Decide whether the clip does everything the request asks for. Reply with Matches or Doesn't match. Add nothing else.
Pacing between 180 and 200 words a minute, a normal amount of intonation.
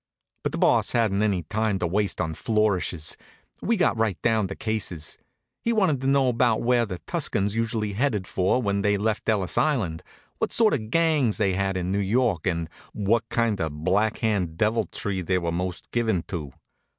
Matches